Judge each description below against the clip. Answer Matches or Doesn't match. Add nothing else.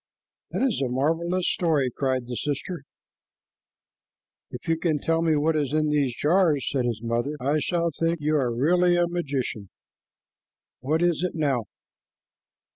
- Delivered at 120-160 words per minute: Matches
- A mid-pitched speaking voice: Matches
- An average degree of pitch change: Matches